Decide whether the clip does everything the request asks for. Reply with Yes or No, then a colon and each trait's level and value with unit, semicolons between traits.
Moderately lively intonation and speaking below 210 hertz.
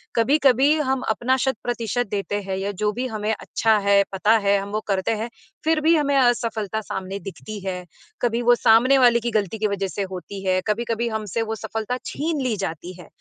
No: average, 3.4 semitones; high, 220 Hz